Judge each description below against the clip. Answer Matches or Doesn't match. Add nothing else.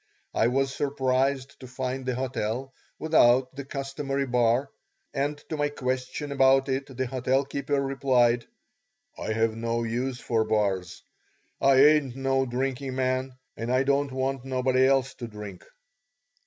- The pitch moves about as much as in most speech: Doesn't match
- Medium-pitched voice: Doesn't match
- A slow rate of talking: Doesn't match